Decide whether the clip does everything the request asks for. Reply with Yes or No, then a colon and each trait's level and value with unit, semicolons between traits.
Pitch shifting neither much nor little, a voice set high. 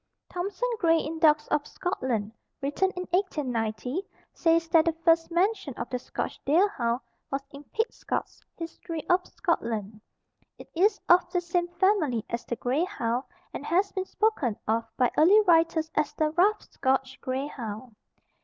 No: wide, 5.9 semitones; very high, 320 Hz